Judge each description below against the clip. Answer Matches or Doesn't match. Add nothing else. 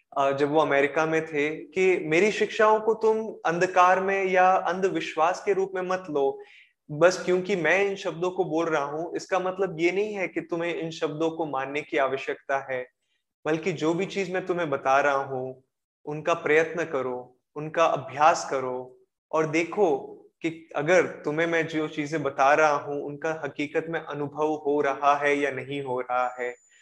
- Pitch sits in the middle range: Matches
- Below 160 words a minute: Doesn't match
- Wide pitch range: Doesn't match